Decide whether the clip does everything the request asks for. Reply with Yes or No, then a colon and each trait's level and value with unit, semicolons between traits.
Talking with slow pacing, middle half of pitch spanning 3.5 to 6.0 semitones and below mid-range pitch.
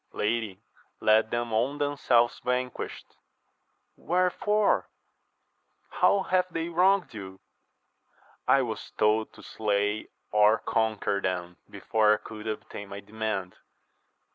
Yes: slow, 115 wpm; average, 5.1 semitones; low, 110 Hz